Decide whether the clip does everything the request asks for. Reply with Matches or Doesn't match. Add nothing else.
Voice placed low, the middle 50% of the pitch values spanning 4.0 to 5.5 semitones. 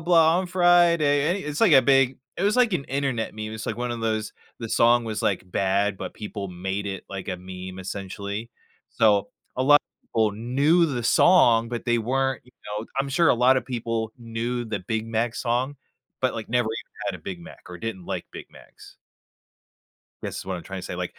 Matches